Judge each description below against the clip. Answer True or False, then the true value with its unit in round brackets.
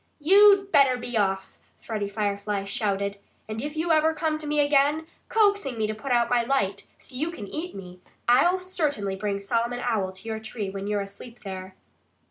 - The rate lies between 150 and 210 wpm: True (190 wpm)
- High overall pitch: True (235 Hz)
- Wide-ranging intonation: True (7.0 semitones)